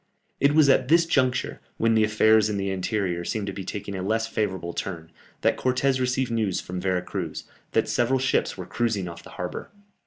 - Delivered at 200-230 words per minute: Yes, fast, 205 wpm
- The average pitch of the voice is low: Yes, low, 105 Hz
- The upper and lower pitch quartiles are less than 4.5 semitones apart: No, average, 5.0 semitones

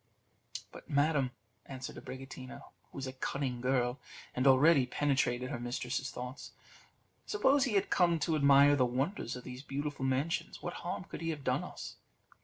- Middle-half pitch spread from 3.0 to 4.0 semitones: No, narrow, 2.5 semitones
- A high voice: No, low, 135 Hz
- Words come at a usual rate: Yes, average, 165 wpm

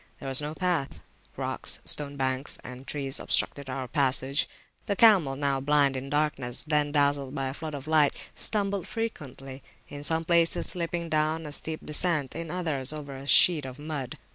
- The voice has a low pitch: No, medium, 145 Hz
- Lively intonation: No, average, 3.0 semitones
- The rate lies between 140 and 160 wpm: No, average, 180 wpm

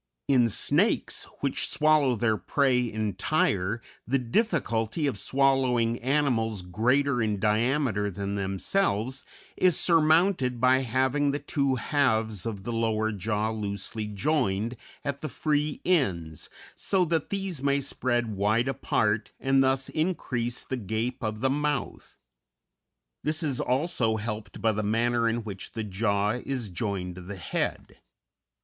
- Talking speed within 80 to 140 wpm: Yes, slow, 135 wpm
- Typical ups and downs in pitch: Yes, average, 4.6 semitones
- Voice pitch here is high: No, low, 120 Hz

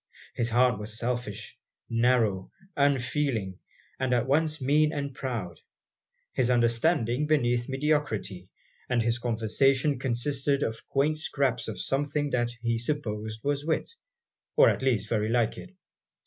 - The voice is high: No, low, 125 Hz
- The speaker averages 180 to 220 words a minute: No, slow, 135 wpm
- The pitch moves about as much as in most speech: Yes, average, 3.7 semitones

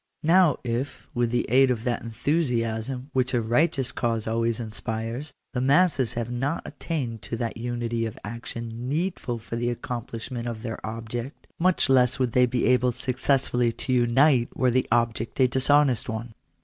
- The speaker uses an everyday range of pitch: No, narrow, 2.2 semitones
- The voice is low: Yes, low, 120 Hz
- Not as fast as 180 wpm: Yes, average, 170 wpm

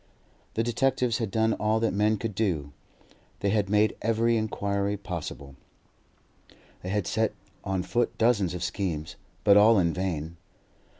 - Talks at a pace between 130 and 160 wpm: Yes, average, 145 wpm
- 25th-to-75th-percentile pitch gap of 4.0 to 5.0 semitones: No, average, 3.5 semitones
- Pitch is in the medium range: No, low, 105 Hz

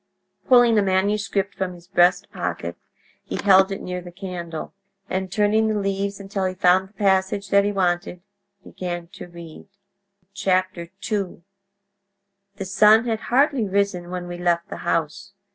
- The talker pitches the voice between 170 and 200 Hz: Yes, high, 190 Hz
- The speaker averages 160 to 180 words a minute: No, average, 150 wpm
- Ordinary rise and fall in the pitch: No, narrow, 2.2 semitones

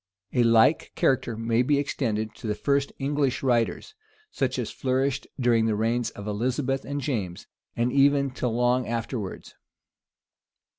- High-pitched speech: No, low, 125 Hz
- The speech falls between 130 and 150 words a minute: Yes, average, 145 wpm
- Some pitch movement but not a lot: Yes, average, 3.2 semitones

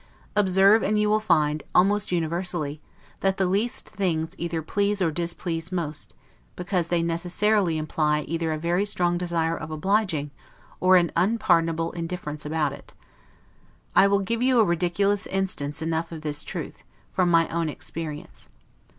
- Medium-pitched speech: Yes, medium, 170 Hz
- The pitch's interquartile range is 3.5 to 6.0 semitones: No, average, 3.1 semitones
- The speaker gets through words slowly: No, average, 150 wpm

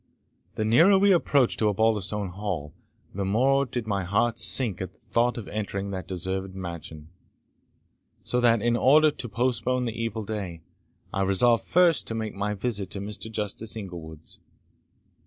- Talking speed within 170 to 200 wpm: No, average, 160 wpm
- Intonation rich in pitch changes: No, average, 3.7 semitones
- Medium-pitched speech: No, low, 105 Hz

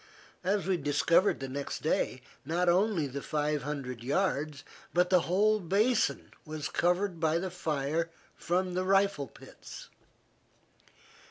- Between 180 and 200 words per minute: No, slow, 135 wpm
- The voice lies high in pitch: No, medium, 170 Hz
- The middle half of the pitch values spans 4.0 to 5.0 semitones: Yes, average, 4.3 semitones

